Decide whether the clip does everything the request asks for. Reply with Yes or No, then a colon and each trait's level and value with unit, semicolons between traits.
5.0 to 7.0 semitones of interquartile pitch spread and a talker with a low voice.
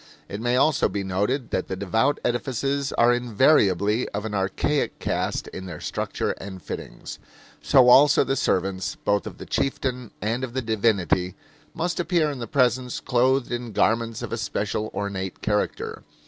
No: average, 4.5 semitones; low, 115 Hz